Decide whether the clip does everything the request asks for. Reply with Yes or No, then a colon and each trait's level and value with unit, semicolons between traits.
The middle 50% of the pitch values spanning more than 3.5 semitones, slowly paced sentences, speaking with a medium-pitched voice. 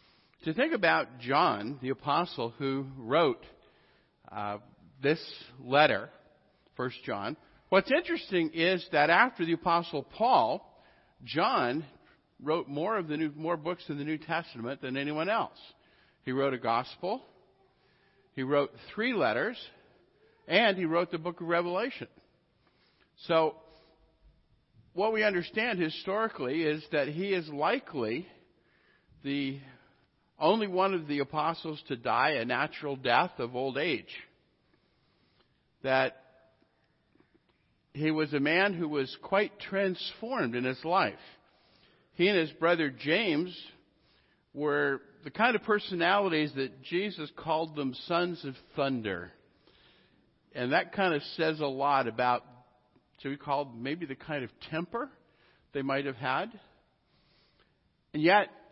Yes: average, 4.4 semitones; slow, 130 wpm; medium, 155 Hz